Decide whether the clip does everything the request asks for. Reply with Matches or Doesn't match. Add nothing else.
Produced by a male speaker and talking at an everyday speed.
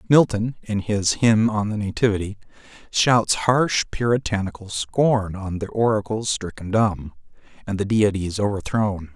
Doesn't match